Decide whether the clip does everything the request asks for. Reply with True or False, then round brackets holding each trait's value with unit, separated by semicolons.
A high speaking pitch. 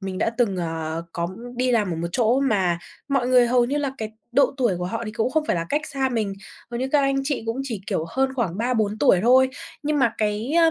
True (235 Hz)